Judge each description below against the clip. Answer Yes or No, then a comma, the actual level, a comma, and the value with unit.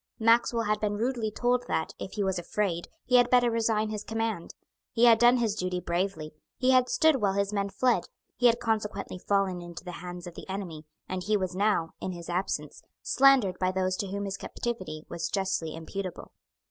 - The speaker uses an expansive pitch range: No, average, 4.0 semitones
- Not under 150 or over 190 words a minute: No, average, 200 wpm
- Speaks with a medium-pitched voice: No, high, 200 Hz